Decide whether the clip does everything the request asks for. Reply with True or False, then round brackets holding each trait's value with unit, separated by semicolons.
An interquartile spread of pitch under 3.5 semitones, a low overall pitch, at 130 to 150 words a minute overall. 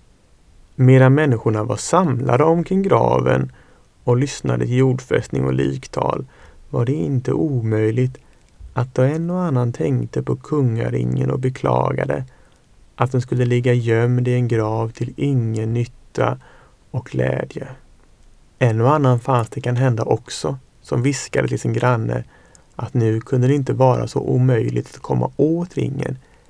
True (3.0 semitones; 125 Hz; 145 wpm)